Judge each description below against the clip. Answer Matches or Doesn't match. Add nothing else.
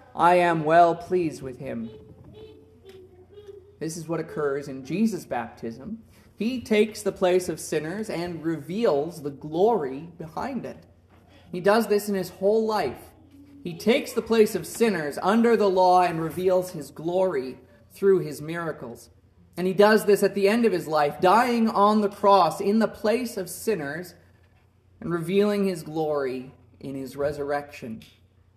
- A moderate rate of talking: Matches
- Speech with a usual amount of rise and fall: Doesn't match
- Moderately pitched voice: Matches